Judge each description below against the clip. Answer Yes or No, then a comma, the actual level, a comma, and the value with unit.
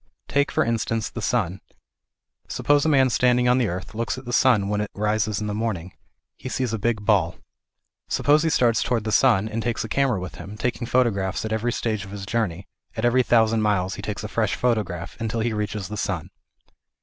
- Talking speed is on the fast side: Yes, fast, 215 wpm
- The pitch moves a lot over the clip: No, average, 3.0 semitones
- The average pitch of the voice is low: Yes, low, 110 Hz